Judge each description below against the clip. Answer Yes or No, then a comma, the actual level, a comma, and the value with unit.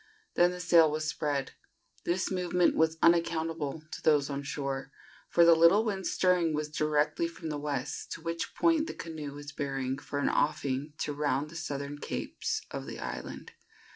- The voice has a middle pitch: Yes, medium, 155 Hz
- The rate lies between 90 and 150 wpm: No, average, 175 wpm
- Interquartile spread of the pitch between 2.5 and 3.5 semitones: Yes, average, 2.9 semitones